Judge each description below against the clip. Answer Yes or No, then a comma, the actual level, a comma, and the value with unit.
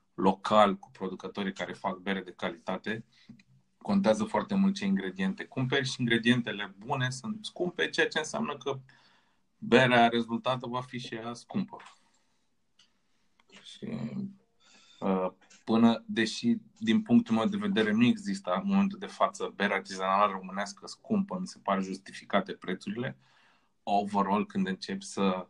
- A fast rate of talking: No, average, 135 wpm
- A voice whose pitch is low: Yes, low, 125 Hz